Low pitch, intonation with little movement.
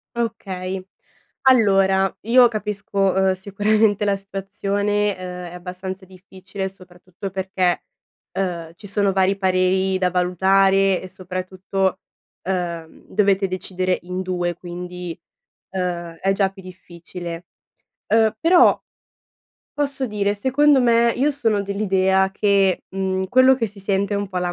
No: high, 190 Hz; narrow, 1.8 semitones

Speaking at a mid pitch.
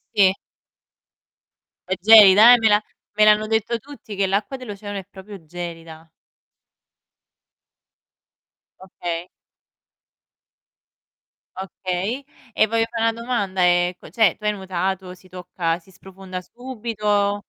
No: high, 200 Hz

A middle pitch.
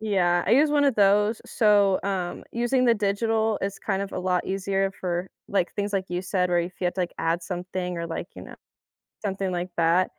No: high, 195 Hz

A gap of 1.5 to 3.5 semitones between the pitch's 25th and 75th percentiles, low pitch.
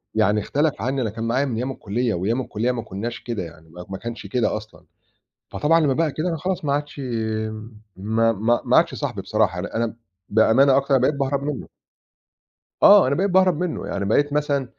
No: average, 4.7 semitones; low, 120 Hz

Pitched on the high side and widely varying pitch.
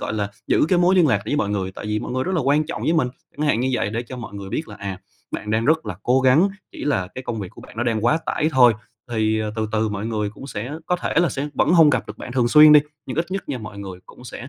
No: low, 120 Hz; wide, 5.8 semitones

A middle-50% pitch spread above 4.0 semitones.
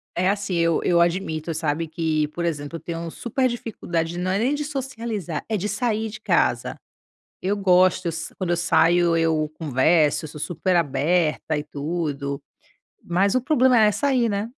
Yes: average, 4.5 semitones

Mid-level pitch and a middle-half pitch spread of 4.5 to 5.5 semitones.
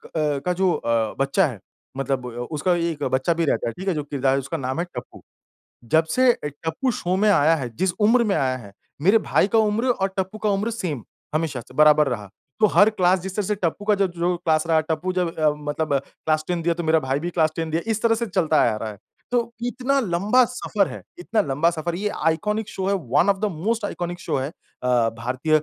Yes: medium, 170 Hz; average, 5.2 semitones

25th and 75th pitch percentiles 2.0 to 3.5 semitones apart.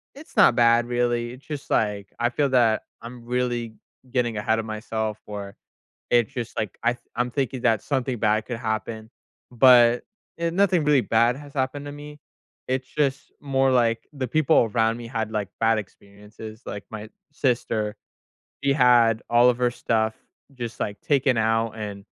Yes: average, 2.8 semitones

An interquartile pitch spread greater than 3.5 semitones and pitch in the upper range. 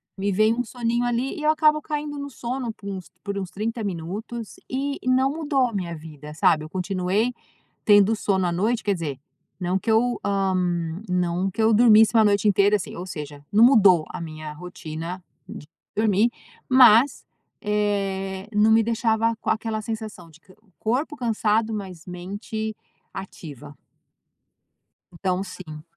Yes: average, 4.0 semitones; high, 205 Hz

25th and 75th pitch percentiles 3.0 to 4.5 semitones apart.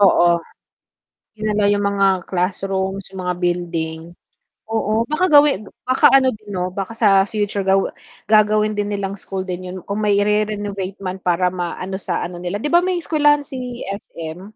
No: narrow, 2.6 semitones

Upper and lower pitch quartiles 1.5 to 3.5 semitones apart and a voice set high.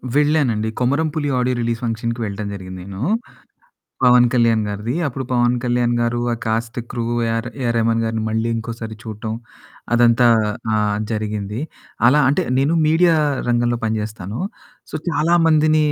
No: narrow, 2.4 semitones; low, 115 Hz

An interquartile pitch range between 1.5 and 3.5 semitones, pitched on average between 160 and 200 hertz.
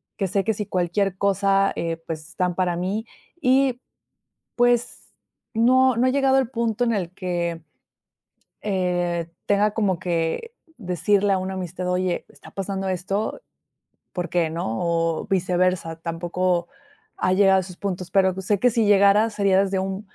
Yes: average, 2.8 semitones; high, 190 Hz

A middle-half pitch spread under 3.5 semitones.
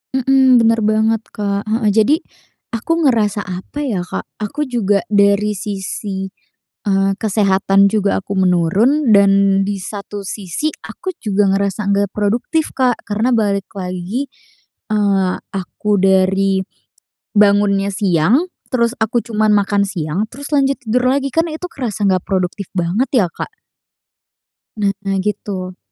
Yes: average, 3.0 semitones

